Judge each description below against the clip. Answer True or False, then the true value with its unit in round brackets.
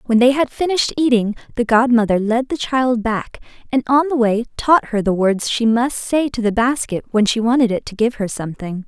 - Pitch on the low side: False (235 Hz)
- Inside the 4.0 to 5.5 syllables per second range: True (5.4 syllables/s)